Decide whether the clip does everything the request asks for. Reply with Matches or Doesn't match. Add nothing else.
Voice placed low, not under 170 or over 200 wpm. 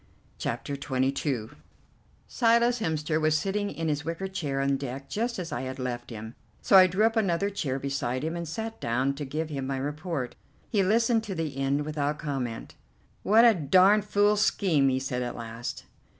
Doesn't match